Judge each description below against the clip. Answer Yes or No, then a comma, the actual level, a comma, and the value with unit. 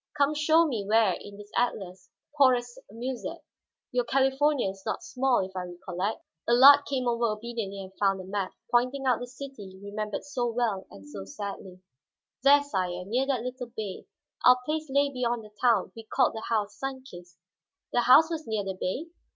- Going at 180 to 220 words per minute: Yes, average, 185 wpm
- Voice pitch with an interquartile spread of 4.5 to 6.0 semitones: Yes, average, 5.2 semitones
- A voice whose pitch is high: Yes, high, 235 Hz